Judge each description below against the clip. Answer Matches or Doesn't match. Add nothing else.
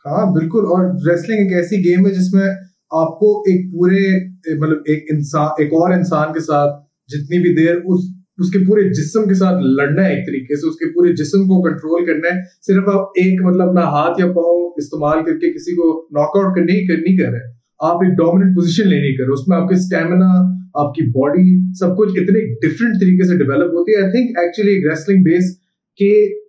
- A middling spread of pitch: Matches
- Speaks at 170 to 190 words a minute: Matches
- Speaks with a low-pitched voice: Doesn't match